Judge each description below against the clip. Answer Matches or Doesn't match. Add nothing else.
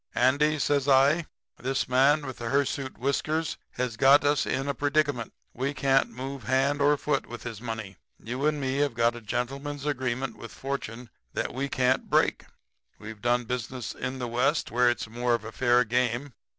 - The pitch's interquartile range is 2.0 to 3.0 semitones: Matches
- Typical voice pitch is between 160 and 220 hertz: Doesn't match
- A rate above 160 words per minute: Matches